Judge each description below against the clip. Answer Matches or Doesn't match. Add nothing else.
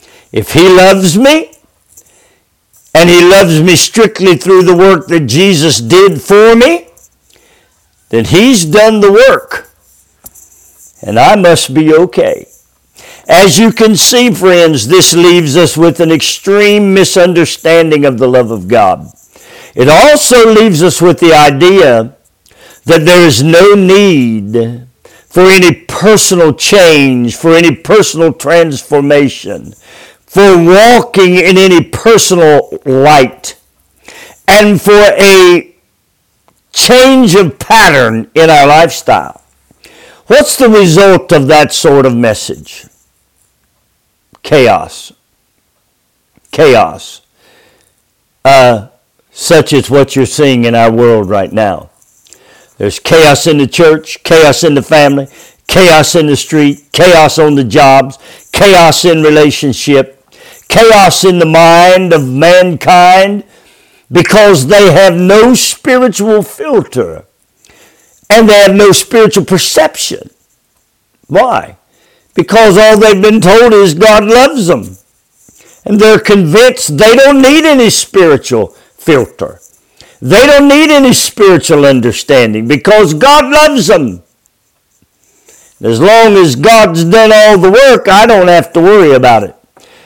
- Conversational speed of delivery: Doesn't match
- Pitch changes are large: Matches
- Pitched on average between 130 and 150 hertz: Doesn't match